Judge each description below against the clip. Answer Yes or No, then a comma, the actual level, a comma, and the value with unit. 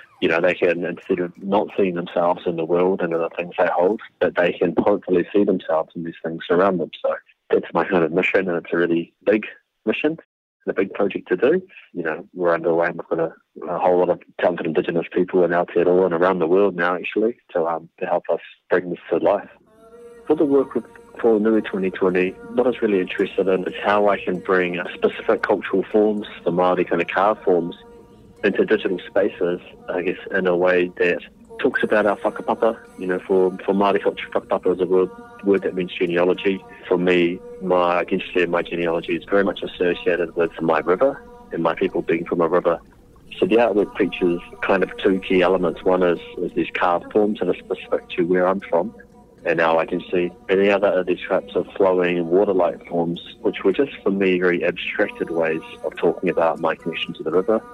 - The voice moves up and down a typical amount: No, narrow, 2.2 semitones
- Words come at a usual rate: No, fast, 215 wpm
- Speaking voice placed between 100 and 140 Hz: No, very low, 90 Hz